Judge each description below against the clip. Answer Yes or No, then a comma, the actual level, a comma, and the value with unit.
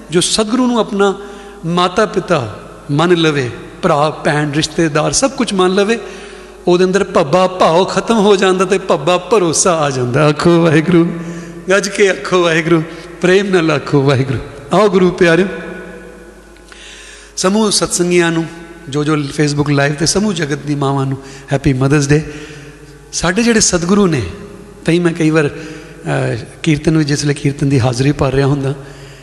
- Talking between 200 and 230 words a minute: No, average, 150 wpm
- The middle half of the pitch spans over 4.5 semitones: No, average, 4.0 semitones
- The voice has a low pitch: No, medium, 165 Hz